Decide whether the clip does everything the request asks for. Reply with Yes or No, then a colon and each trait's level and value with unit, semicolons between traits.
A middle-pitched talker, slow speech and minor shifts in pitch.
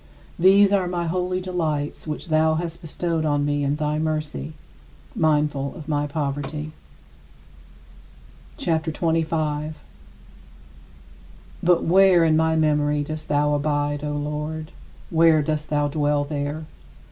Yes: medium, 155 Hz; slow, 125 wpm; narrow, 1.8 semitones